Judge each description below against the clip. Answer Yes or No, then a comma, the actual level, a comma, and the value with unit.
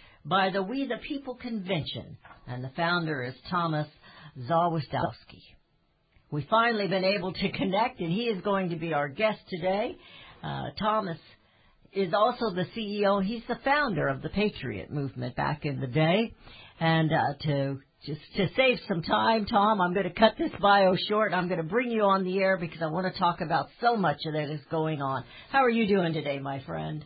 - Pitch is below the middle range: No, medium, 180 Hz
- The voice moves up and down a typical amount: No, wide, 5.9 semitones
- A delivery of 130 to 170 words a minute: No, average, 195 wpm